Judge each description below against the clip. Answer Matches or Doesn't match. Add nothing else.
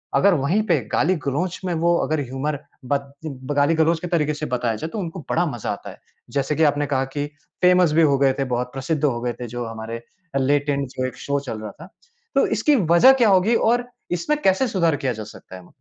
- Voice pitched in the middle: Matches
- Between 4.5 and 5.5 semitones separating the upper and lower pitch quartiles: Matches